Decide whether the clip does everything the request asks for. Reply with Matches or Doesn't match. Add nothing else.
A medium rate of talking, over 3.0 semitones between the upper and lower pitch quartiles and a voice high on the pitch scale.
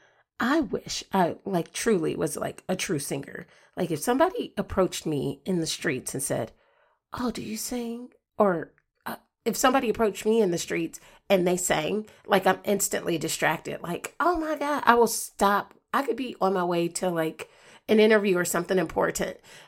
Matches